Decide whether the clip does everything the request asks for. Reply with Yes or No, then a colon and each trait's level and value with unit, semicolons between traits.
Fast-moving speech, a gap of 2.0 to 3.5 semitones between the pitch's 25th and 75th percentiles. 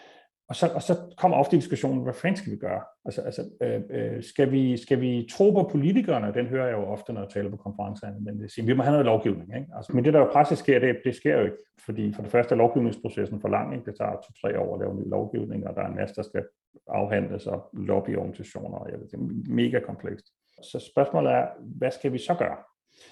No: fast, 245 wpm; average, 5.2 semitones